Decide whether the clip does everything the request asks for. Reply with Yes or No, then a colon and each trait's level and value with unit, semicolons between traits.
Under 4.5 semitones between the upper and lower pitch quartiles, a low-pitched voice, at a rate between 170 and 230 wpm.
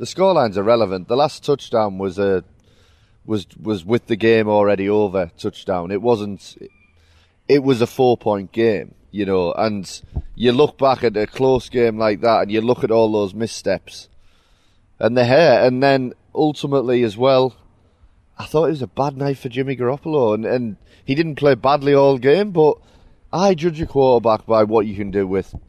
No: average, 4.8 semitones; low, 115 Hz; average, 190 wpm